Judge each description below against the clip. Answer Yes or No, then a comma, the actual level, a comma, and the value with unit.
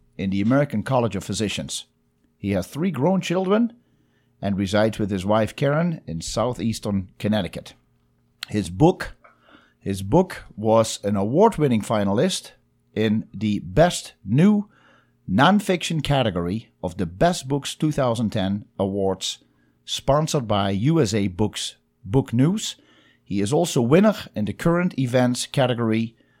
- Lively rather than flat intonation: Yes, wide, 6.9 semitones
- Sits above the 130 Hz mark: No, low, 110 Hz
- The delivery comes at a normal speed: No, slow, 125 wpm